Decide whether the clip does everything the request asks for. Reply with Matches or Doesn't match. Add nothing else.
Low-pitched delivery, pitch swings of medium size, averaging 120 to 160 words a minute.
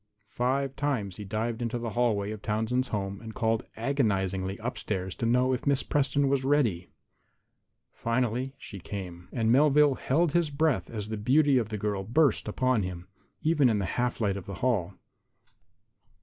Doesn't match